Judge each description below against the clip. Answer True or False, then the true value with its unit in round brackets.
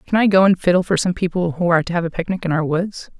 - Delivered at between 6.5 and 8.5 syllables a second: True (7.0 syllables/s)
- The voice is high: False (175 Hz)